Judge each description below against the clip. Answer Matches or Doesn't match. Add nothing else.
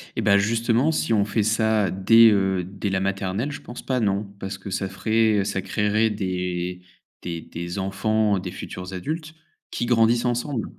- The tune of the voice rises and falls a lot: Doesn't match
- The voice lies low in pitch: Matches